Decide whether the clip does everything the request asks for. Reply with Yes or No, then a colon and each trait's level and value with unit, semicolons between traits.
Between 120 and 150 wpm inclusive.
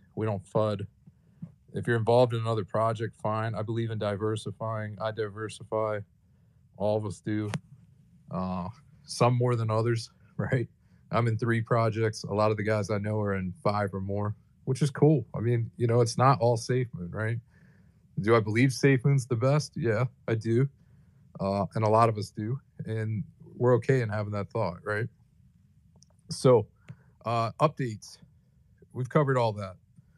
No: average, 175 wpm